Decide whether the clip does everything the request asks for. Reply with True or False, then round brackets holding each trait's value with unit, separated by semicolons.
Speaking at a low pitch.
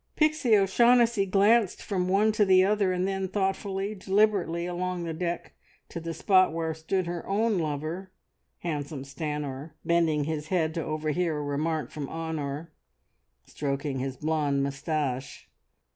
False (170 Hz)